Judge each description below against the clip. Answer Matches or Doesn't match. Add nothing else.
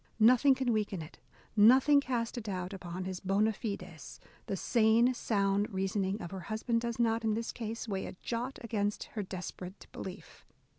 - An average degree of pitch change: Matches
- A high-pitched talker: Matches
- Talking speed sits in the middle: Matches